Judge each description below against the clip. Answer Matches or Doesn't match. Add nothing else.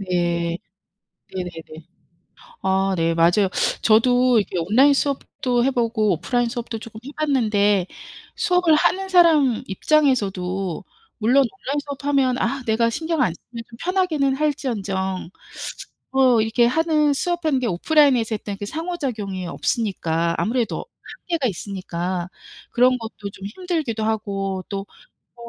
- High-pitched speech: Matches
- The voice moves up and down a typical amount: Doesn't match